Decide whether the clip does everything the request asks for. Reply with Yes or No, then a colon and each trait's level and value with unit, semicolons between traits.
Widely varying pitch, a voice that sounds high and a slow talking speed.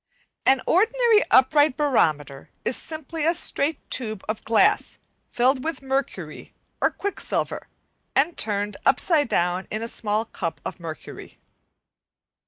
Yes: wide, 7.1 semitones; very high, 260 Hz; slow, 125 wpm